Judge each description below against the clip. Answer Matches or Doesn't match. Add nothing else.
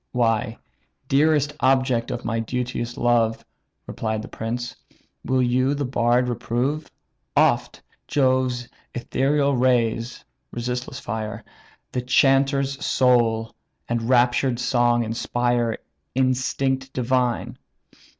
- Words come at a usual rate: Doesn't match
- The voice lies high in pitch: Doesn't match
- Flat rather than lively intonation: Matches